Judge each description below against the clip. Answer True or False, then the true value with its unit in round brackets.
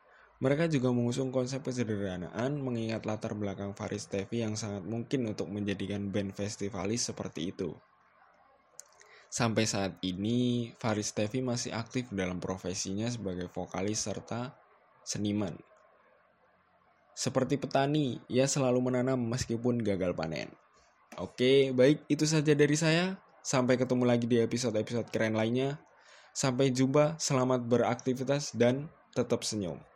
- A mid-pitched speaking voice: False (120 Hz)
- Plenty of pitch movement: False (4.0 semitones)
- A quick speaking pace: False (120 wpm)